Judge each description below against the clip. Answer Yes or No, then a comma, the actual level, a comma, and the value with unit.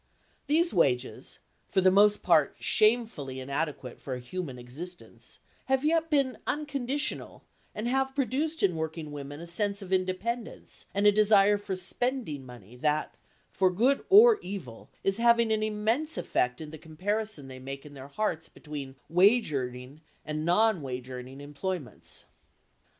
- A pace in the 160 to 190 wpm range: No, average, 150 wpm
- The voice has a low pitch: No, medium, 185 Hz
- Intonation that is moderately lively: No, wide, 8.0 semitones